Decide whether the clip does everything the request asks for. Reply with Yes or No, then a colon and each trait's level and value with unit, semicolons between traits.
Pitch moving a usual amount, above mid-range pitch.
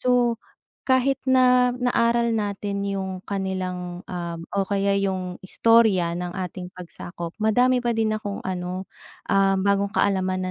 Yes: average, 3.8 semitones; high, 200 Hz